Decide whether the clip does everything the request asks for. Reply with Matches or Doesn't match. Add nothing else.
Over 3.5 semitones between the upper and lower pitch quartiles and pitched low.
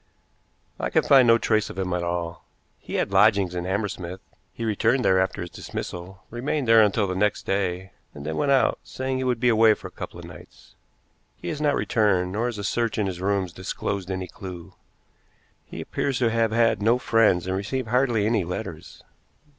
Matches